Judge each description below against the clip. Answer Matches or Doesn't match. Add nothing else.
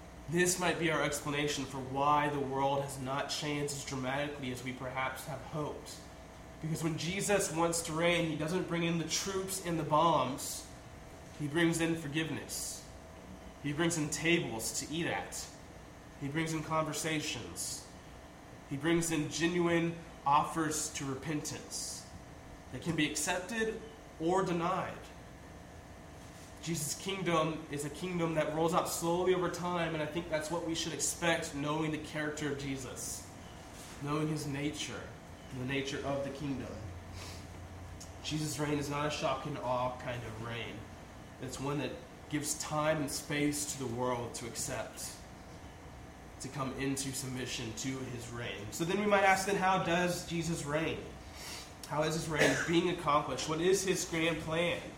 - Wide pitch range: Doesn't match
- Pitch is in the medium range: Matches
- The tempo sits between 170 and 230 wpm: Doesn't match